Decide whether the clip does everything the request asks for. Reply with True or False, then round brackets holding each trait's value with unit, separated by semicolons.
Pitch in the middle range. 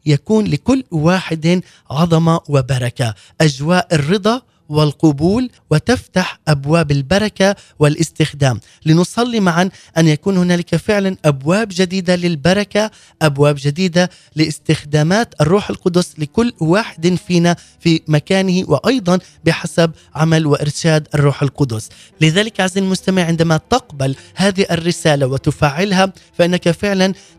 True (170 Hz)